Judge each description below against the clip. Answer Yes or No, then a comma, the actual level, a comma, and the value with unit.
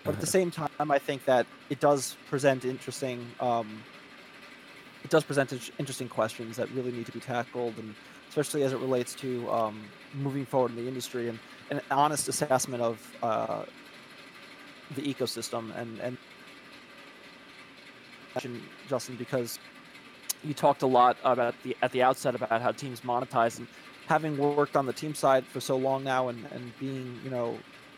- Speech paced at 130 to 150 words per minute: No, average, 165 wpm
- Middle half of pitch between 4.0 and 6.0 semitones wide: No, average, 2.7 semitones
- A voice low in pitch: Yes, low, 130 Hz